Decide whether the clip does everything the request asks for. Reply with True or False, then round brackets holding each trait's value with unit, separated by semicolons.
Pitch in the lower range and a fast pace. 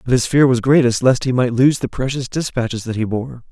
True (125 Hz; 255 wpm)